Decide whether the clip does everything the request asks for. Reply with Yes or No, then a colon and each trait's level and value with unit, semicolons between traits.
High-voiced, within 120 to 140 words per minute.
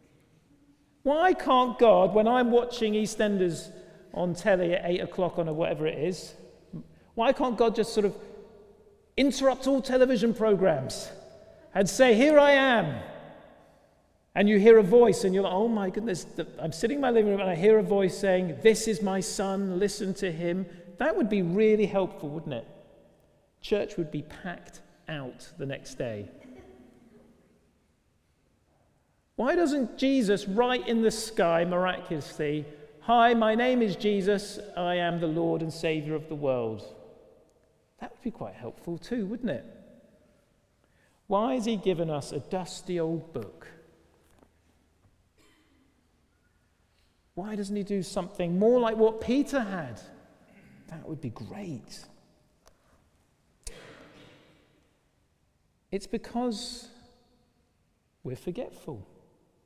Yes: high, 195 Hz; slow, 135 wpm